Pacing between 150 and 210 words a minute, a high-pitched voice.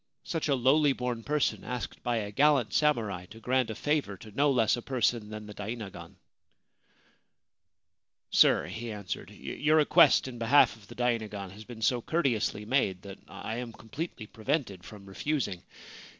No: average, 175 wpm; low, 115 Hz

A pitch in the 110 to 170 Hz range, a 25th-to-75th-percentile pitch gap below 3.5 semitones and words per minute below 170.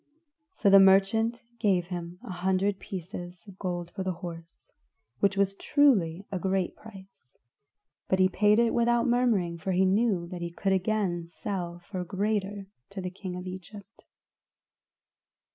No: high, 190 Hz; narrow, 2.4 semitones; average, 160 wpm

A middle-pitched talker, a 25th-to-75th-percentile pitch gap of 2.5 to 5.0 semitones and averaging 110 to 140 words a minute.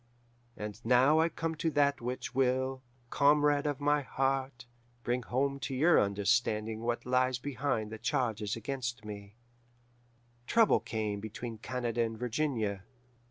No: low, 125 Hz; average, 4.0 semitones; slow, 135 wpm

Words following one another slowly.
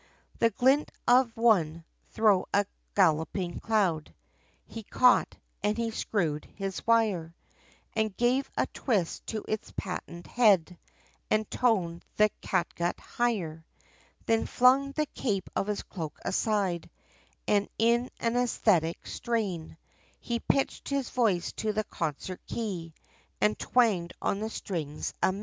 Yes: slow, 130 wpm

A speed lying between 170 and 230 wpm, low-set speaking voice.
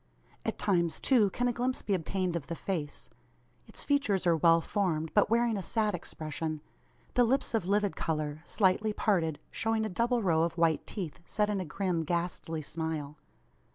No: average, 180 wpm; medium, 180 Hz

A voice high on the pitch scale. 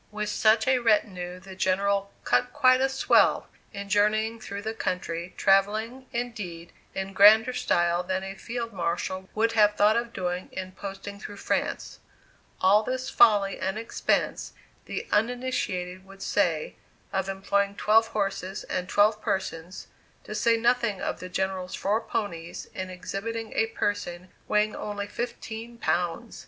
Yes: high, 200 Hz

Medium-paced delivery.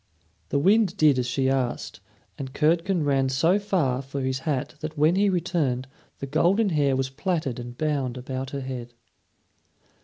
Yes: average, 165 wpm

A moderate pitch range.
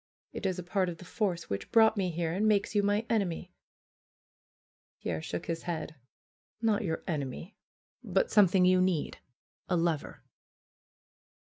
Yes: average, 3.5 semitones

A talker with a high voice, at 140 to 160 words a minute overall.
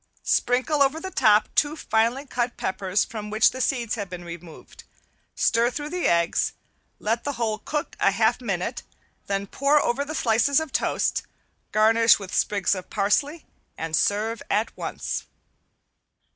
Yes: high, 225 Hz; average, 155 wpm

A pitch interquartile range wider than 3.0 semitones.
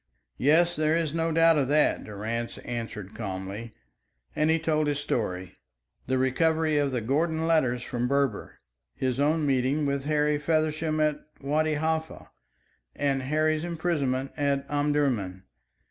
Yes: average, 3.5 semitones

